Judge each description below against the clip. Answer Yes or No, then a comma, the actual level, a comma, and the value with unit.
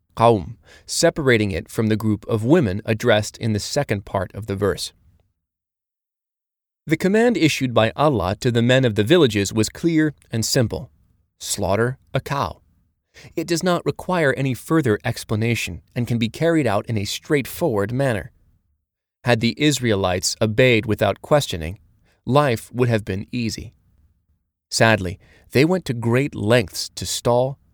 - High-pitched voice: No, low, 110 Hz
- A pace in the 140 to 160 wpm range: Yes, average, 145 wpm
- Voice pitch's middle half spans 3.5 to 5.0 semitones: Yes, average, 4.7 semitones